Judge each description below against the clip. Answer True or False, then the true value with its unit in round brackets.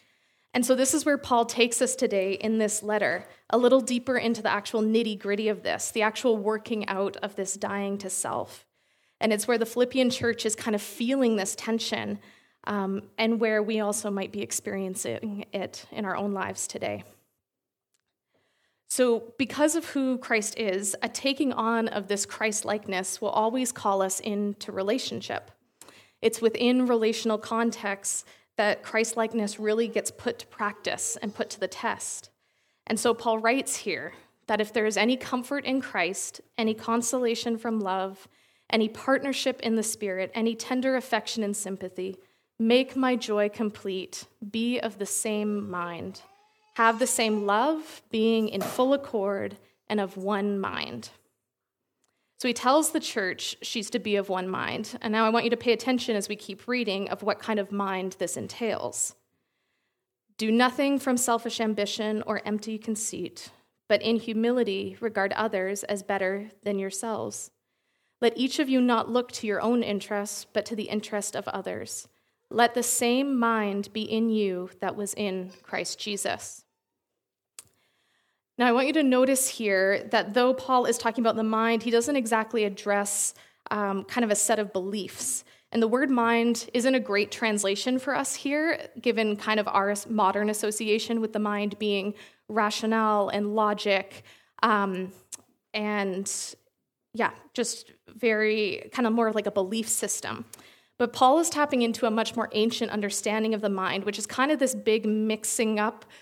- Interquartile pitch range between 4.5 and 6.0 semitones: False (2.6 semitones)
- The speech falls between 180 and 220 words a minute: False (170 wpm)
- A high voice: True (220 Hz)